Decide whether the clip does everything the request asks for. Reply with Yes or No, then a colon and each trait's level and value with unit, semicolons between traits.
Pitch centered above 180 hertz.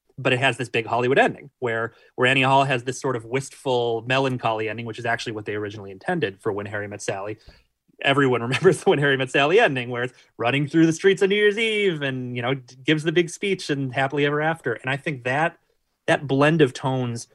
No: low, 130 Hz